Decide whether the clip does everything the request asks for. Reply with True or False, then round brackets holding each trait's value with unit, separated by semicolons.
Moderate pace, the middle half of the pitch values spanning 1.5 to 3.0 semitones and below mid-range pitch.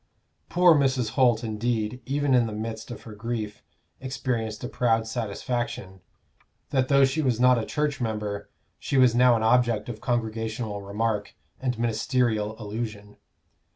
True (150 wpm; 2.6 semitones; 115 Hz)